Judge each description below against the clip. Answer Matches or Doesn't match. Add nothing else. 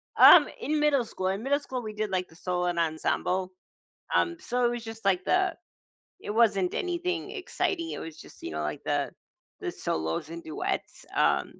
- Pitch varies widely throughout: Matches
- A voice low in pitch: Doesn't match